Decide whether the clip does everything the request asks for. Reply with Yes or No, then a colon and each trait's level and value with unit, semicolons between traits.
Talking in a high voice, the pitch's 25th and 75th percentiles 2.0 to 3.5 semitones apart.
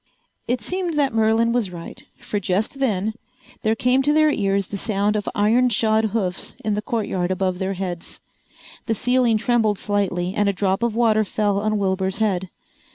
Yes: high, 210 Hz; average, 3.1 semitones